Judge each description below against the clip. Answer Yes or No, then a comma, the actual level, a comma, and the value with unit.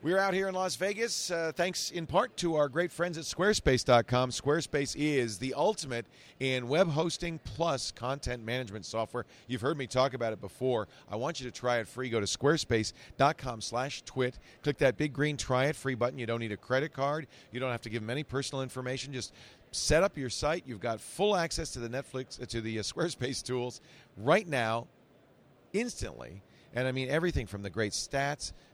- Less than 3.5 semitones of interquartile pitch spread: No, average, 4.3 semitones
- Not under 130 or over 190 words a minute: No, fast, 205 wpm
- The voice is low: Yes, low, 130 Hz